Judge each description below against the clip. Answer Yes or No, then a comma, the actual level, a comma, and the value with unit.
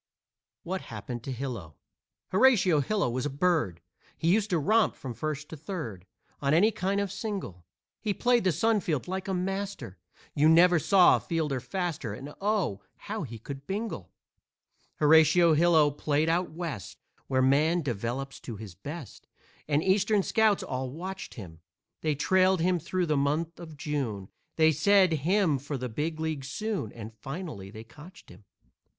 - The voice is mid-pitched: Yes, medium, 155 Hz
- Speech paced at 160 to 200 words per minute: Yes, average, 165 wpm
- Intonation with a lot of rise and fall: Yes, wide, 5.9 semitones